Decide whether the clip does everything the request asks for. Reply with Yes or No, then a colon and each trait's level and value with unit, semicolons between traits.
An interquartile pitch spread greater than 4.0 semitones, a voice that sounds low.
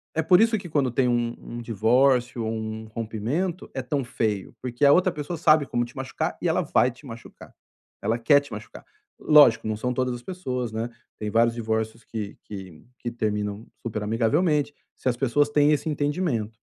Yes: average, 4.6 semitones; low, 120 Hz